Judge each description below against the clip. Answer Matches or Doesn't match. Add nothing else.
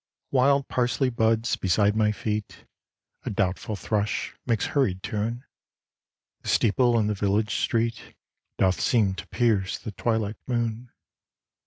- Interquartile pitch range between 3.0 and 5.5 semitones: Doesn't match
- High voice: Doesn't match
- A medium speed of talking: Doesn't match